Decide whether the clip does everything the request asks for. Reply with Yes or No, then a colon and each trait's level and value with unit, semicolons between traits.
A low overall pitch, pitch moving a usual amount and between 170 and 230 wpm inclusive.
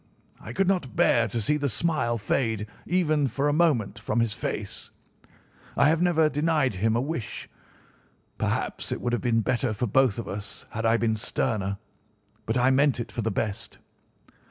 Yes: low, 120 Hz; average, 4.9 semitones; average, 180 wpm